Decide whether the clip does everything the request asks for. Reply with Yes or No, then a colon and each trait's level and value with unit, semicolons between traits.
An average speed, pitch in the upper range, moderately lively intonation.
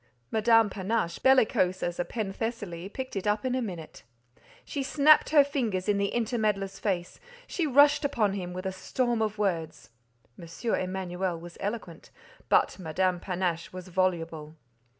Yes: average, 150 wpm; high, 195 Hz; average, 4.6 semitones